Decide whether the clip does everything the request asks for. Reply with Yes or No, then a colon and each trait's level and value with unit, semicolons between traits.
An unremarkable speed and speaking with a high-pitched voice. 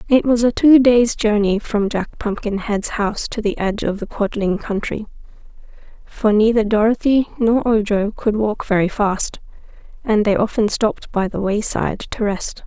Yes: average, 165 wpm; high, 215 Hz